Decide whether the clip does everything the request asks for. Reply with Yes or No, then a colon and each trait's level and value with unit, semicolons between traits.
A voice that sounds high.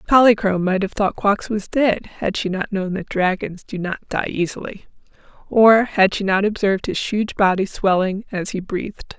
Yes: high, 200 Hz